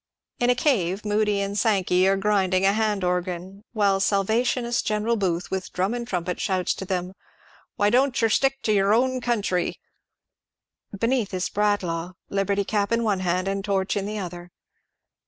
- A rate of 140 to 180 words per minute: Yes, average, 175 wpm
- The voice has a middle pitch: No, high, 200 Hz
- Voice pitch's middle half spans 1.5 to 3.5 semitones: Yes, average, 2.7 semitones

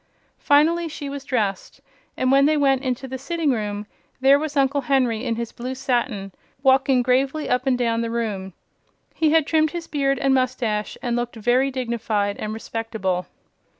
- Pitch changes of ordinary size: Yes, average, 3.4 semitones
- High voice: Yes, very high, 255 Hz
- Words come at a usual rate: Yes, average, 175 wpm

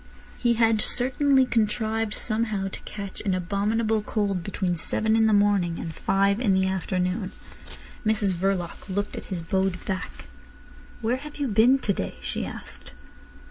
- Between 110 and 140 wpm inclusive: No, average, 155 wpm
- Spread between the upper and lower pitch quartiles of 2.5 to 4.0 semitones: Yes, average, 2.9 semitones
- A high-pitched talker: Yes, high, 205 Hz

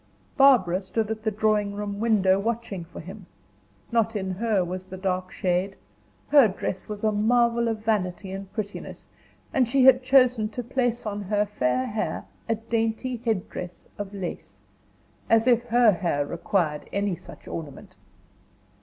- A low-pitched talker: No, high, 210 Hz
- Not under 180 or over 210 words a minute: No, average, 155 wpm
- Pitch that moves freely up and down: No, average, 3.5 semitones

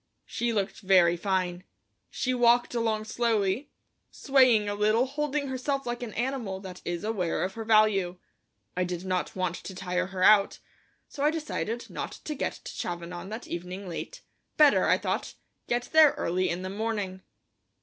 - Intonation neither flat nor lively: Yes, average, 4.8 semitones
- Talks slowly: No, average, 170 wpm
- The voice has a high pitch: Yes, high, 210 Hz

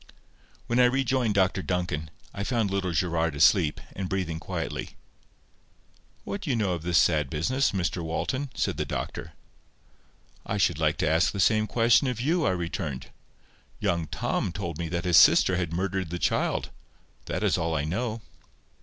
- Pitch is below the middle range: Yes, very low, 90 Hz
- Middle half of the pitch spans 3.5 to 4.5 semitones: No, average, 5.1 semitones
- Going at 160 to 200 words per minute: Yes, average, 170 wpm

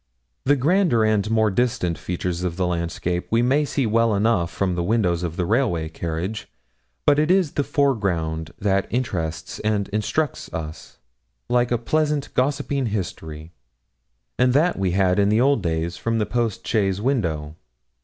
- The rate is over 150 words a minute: Yes, average, 160 wpm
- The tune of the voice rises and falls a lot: Yes, wide, 6.2 semitones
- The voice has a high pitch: No, low, 105 Hz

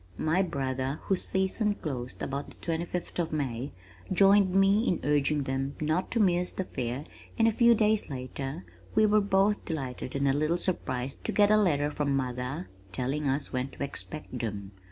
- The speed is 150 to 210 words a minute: Yes, average, 185 wpm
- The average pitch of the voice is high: No, medium, 150 Hz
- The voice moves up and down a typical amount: No, wide, 6.1 semitones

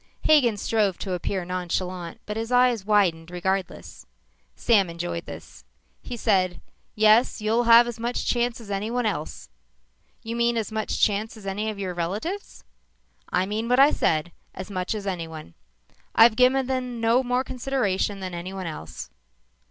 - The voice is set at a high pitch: Yes, high, 210 Hz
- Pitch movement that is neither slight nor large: Yes, average, 4.4 semitones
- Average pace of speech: Yes, average, 160 wpm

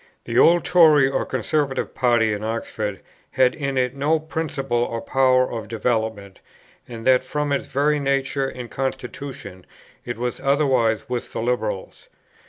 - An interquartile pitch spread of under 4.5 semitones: Yes, average, 3.2 semitones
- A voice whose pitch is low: Yes, low, 130 Hz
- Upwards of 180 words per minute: No, average, 150 wpm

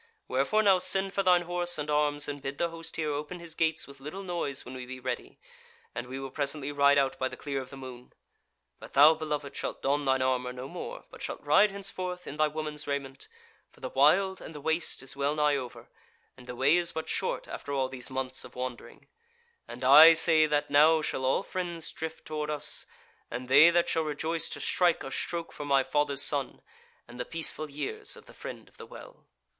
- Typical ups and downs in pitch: Yes, average, 3.4 semitones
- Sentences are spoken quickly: Yes, fast, 220 wpm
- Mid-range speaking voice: Yes, medium, 145 Hz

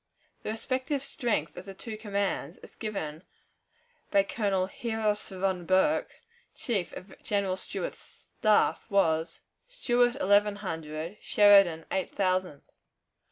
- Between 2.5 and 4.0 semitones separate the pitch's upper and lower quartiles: Yes, average, 3.0 semitones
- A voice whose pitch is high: Yes, high, 200 Hz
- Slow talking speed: Yes, slow, 115 wpm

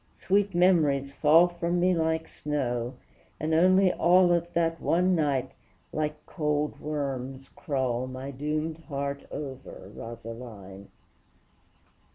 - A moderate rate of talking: No, slow, 115 wpm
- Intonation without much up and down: No, average, 4.3 semitones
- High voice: No, medium, 150 Hz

